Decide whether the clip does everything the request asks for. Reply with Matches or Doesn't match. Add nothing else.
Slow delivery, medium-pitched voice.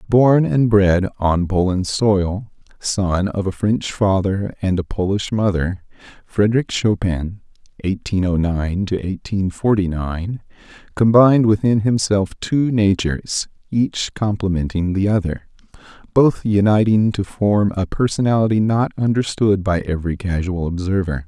Doesn't match